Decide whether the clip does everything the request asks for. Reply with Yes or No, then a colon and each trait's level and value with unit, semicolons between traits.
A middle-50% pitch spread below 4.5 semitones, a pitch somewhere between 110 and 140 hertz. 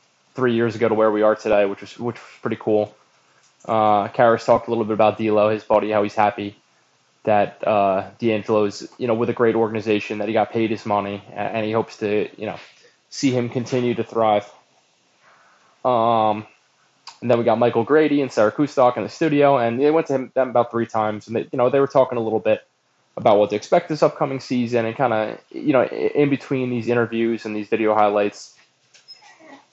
Yes: narrow, 2.5 semitones; low, 115 Hz